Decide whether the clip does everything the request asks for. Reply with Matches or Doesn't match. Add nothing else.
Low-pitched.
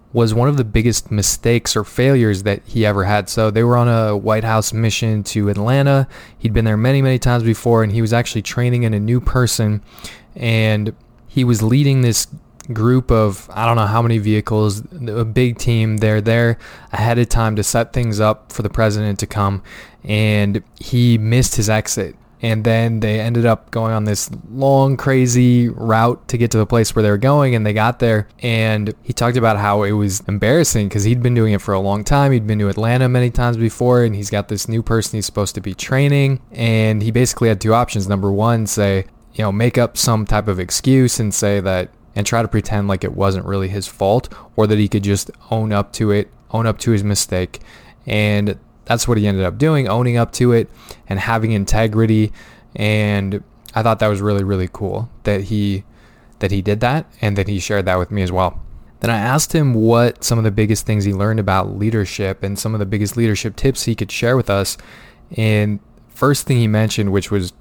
Matches